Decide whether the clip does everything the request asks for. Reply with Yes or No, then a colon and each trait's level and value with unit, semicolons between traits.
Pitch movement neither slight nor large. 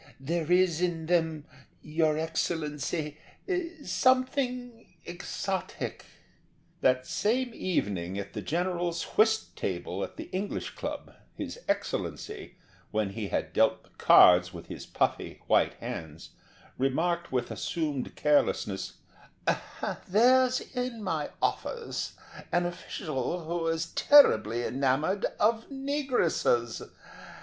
No: wide, 8.3 semitones